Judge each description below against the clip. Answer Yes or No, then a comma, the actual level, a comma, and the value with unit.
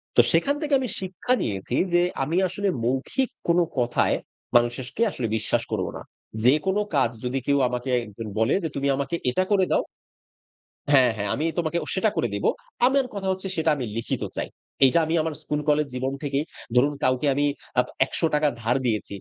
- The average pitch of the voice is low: No, medium, 145 Hz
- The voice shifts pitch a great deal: Yes, wide, 5.9 semitones